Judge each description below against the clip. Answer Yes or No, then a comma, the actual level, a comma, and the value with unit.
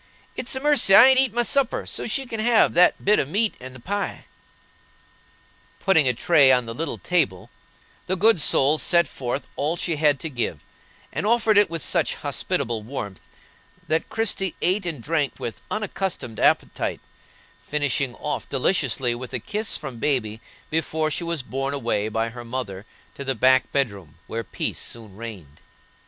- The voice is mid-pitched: Yes, medium, 145 Hz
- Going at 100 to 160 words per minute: No, average, 175 wpm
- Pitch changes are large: Yes, wide, 8.1 semitones